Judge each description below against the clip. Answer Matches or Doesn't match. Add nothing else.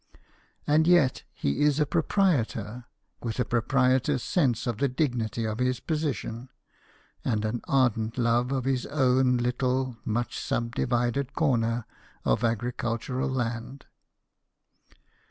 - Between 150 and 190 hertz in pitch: Doesn't match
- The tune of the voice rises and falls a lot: Doesn't match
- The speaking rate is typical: Doesn't match